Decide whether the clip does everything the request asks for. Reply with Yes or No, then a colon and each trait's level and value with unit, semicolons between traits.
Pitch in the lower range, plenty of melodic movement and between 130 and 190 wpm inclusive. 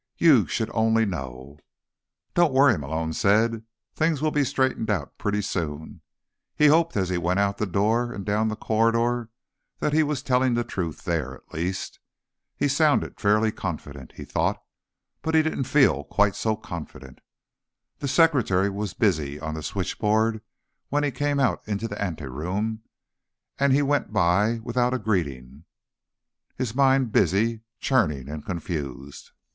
Yes: low, 105 Hz; wide, 6.7 semitones; average, 155 wpm